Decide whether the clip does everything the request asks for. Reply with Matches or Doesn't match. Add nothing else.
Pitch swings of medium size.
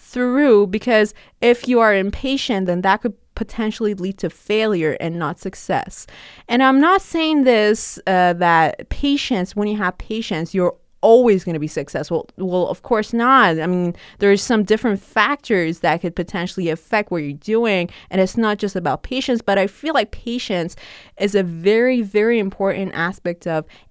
Matches